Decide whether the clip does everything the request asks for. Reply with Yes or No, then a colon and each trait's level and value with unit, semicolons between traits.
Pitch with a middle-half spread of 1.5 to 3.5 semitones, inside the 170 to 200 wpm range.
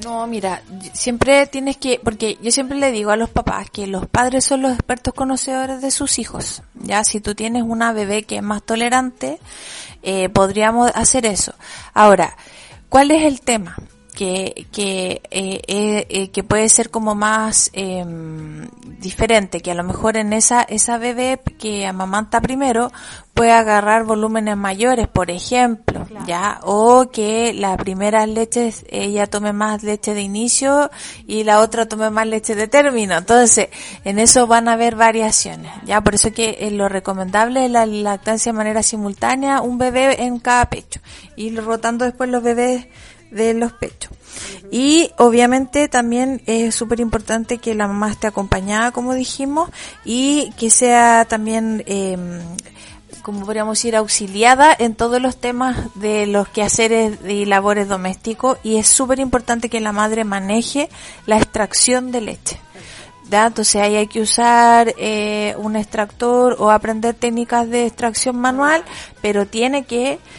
No: average, 2.7 semitones; average, 160 wpm